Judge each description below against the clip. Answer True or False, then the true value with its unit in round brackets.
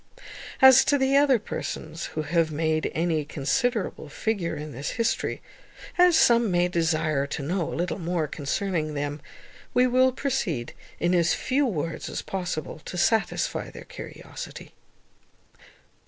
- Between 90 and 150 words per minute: True (140 wpm)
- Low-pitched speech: False (175 Hz)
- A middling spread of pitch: False (7.4 semitones)